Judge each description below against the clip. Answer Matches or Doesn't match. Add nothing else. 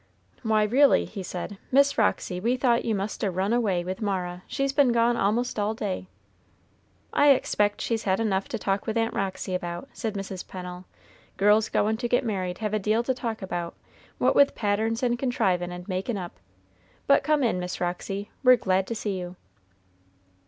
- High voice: Matches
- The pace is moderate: Matches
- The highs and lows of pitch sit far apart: Doesn't match